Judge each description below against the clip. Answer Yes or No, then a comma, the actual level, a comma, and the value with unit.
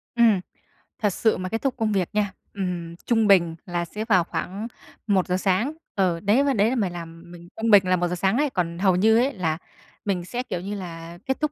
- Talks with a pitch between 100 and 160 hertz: No, high, 190 Hz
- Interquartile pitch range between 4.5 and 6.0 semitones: No, average, 4.1 semitones